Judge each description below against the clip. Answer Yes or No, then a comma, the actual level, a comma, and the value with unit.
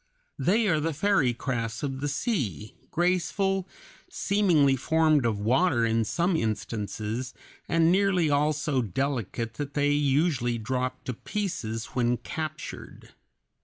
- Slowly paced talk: Yes, slow, 130 wpm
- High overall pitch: No, medium, 140 Hz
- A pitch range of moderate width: No, wide, 6.1 semitones